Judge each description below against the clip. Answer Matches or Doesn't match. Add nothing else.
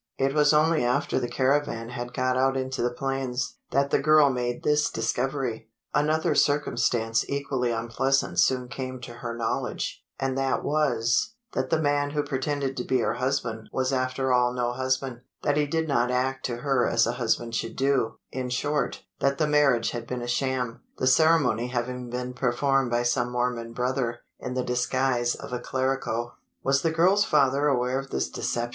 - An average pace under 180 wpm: Doesn't match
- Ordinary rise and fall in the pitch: Doesn't match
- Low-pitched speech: Matches